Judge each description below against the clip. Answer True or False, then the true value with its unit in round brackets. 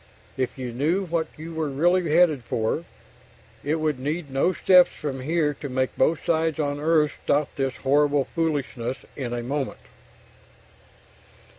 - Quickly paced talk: False (150 wpm)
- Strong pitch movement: False (3.3 semitones)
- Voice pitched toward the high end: False (150 Hz)